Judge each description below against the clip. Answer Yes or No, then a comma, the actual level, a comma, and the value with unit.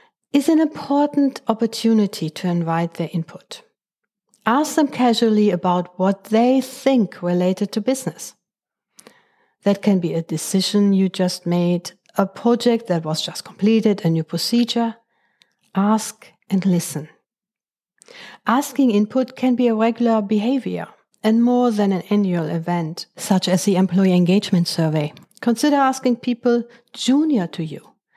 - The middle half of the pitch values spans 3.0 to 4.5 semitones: No, average, 5.1 semitones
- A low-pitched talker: No, high, 215 Hz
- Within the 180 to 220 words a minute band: No, slow, 135 wpm